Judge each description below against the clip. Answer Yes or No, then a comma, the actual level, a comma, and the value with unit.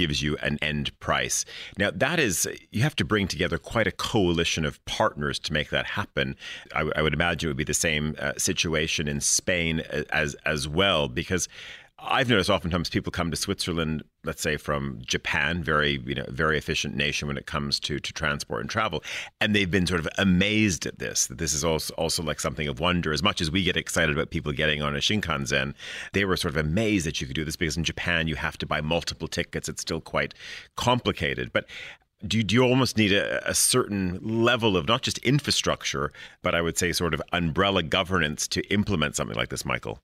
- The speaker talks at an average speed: No, fast, 215 wpm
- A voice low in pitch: Yes, very low, 85 Hz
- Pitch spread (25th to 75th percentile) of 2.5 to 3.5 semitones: No, average, 4.2 semitones